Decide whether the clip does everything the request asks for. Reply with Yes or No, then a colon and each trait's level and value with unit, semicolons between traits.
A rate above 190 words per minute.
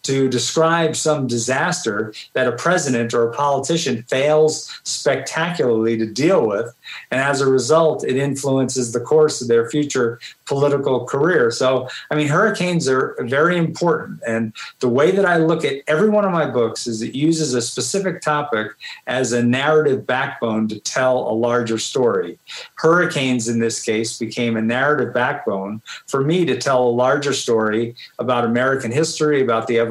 No: average, 165 wpm